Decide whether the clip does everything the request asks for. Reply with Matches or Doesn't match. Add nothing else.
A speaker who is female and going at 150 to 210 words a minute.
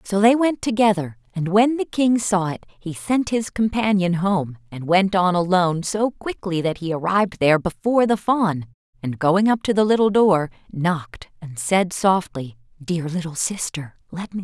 Matches